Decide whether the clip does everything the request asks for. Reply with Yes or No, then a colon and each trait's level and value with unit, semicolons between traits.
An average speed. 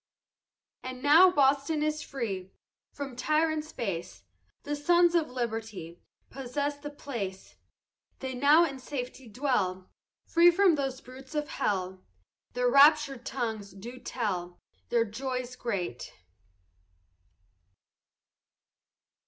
No: slow, 105 wpm